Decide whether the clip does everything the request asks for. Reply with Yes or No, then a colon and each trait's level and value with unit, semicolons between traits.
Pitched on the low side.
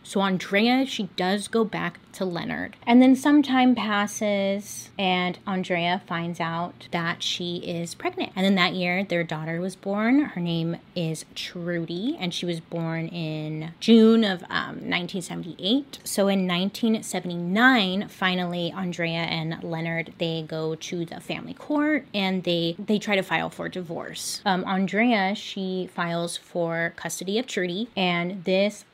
No: medium, 185 Hz